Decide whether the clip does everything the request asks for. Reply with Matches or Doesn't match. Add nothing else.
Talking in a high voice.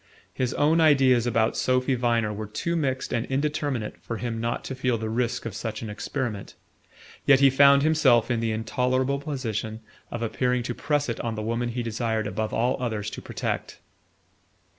Doesn't match